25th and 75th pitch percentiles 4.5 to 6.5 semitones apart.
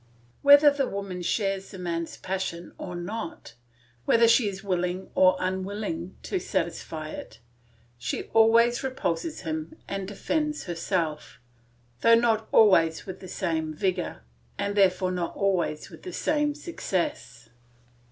Yes: average, 4.8 semitones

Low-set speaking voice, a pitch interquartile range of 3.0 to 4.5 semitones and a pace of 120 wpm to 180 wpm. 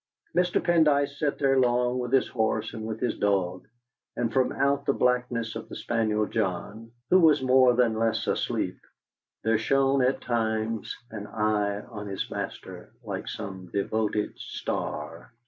Yes: low, 115 Hz; average, 3.6 semitones; average, 160 wpm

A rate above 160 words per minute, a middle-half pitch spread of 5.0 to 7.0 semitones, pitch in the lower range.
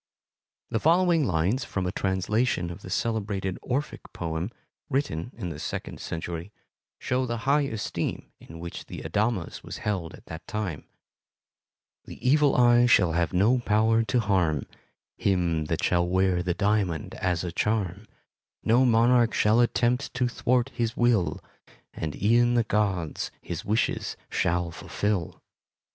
No: average, 145 wpm; wide, 5.4 semitones; low, 105 Hz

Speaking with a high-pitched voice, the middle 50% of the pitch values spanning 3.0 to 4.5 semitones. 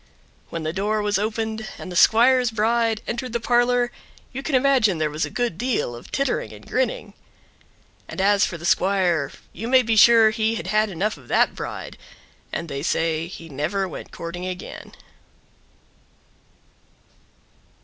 No: high, 215 Hz; average, 5.2 semitones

